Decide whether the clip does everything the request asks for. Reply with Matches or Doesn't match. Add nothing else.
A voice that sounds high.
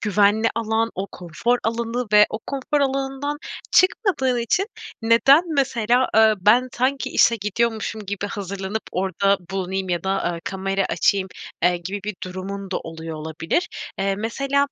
Matches